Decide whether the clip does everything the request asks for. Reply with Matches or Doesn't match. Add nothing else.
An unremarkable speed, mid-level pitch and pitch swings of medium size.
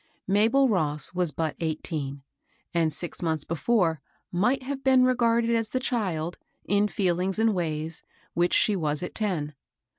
Doesn't match